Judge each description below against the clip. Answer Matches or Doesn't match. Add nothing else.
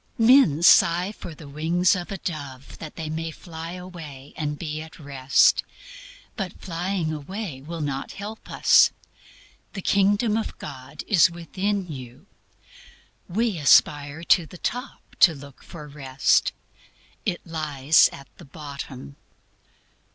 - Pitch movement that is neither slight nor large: Matches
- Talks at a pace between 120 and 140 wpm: Matches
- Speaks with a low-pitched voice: Doesn't match